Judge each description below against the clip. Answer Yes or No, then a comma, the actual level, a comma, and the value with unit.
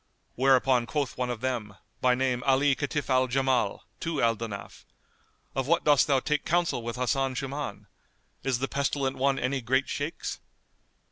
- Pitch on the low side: Yes, low, 130 Hz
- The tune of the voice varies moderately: No, narrow, 2.1 semitones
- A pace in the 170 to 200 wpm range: No, average, 160 wpm